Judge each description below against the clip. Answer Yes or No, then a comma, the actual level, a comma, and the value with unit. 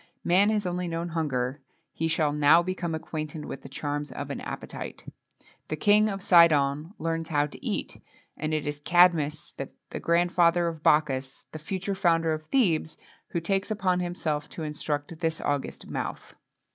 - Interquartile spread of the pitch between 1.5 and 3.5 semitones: Yes, average, 2.9 semitones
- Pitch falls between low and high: Yes, medium, 160 Hz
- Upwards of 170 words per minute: No, average, 165 wpm